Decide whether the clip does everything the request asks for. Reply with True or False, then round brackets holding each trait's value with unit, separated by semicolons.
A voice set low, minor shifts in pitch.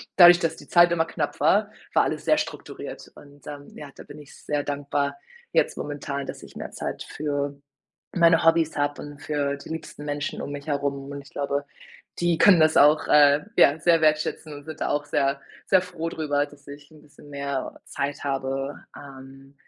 False (145 Hz; 1.9 semitones)